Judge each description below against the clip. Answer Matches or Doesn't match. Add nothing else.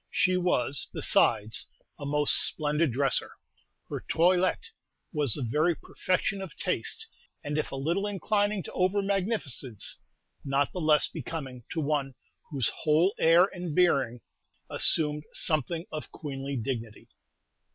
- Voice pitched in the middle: Matches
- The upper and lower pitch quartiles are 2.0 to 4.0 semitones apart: Doesn't match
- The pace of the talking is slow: Matches